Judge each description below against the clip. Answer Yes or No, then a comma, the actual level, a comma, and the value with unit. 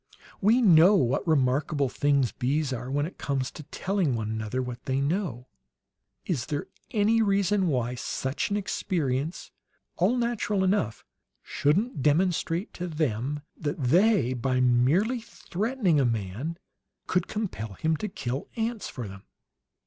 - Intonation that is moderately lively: No, wide, 7.4 semitones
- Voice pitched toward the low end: No, medium, 150 Hz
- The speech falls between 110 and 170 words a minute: Yes, average, 140 wpm